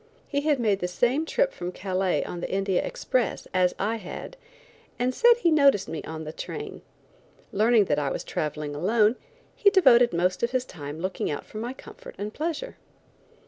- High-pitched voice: Yes, high, 215 Hz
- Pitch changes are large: Yes, wide, 7.1 semitones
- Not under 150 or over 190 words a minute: Yes, average, 185 wpm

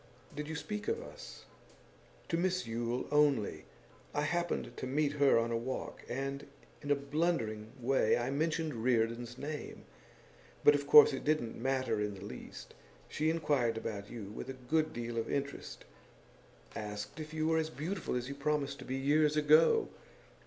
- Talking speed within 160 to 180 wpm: Yes, average, 170 wpm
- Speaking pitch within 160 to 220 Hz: No, medium, 140 Hz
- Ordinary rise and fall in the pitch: Yes, average, 4.5 semitones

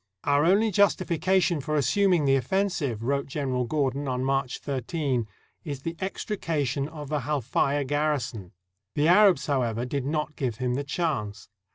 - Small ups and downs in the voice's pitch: No, average, 4.0 semitones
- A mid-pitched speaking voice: Yes, medium, 145 Hz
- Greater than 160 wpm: No, average, 150 wpm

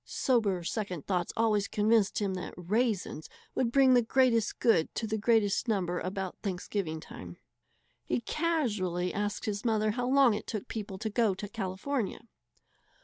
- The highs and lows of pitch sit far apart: No, average, 3.6 semitones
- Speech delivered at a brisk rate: No, average, 155 wpm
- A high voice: Yes, high, 210 Hz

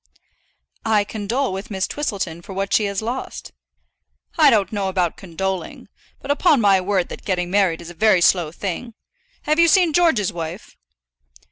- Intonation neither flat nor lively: Yes, average, 4.1 semitones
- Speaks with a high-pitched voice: Yes, high, 200 Hz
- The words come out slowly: No, average, 165 wpm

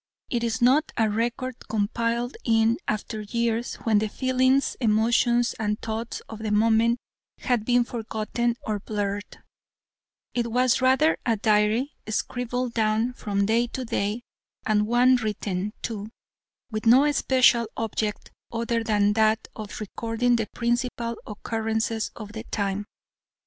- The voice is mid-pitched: No, high, 225 Hz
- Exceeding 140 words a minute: No, slow, 135 wpm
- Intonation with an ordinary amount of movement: No, narrow, 2.1 semitones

